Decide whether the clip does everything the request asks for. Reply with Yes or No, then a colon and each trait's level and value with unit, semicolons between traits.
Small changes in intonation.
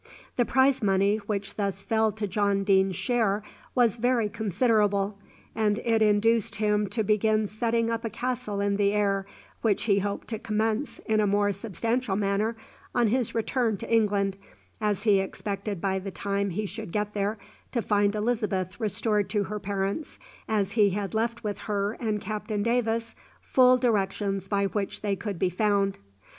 Yes: narrow, 2.0 semitones